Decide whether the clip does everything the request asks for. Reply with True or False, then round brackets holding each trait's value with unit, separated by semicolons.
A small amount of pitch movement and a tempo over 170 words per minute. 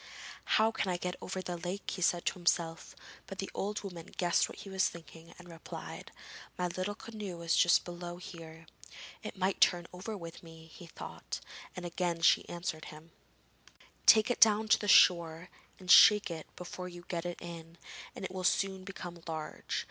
True (2.1 semitones; 185 wpm)